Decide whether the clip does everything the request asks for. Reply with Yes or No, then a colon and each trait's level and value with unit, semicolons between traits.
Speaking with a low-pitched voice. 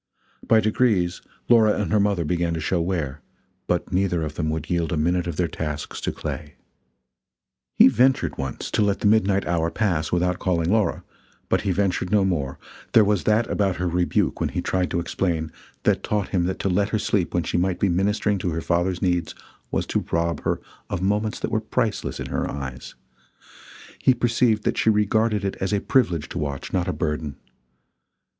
Yes: very low, 90 Hz